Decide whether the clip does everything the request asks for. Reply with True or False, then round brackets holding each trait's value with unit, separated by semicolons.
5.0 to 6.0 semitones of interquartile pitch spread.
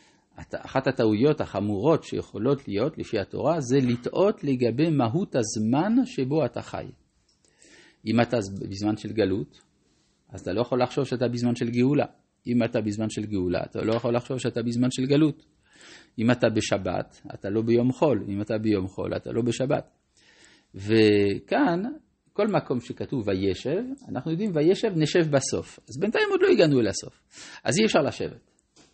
True (5.3 semitones)